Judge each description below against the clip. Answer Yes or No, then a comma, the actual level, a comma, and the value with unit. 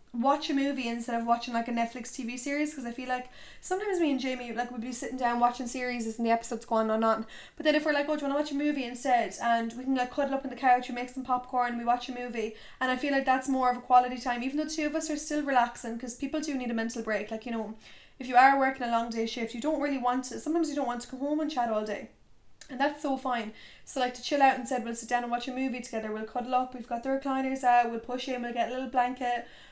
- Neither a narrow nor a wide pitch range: No, narrow, 2.2 semitones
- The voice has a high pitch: Yes, very high, 250 Hz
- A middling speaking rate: No, fast, 310 wpm